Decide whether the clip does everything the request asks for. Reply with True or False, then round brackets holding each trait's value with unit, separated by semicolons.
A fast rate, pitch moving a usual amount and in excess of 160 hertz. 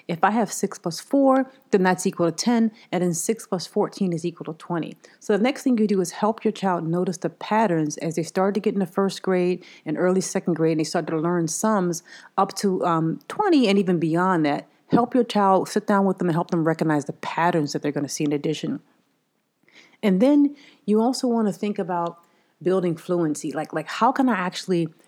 True (225 wpm; 4.0 semitones; 185 Hz)